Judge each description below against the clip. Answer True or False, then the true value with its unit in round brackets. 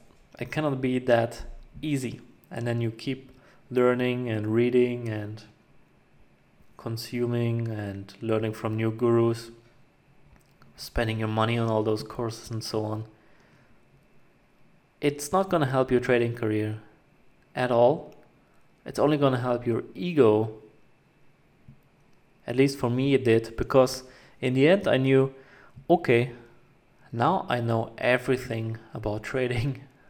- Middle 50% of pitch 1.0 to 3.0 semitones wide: True (2.6 semitones)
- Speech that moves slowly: True (130 wpm)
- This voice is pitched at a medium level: False (120 Hz)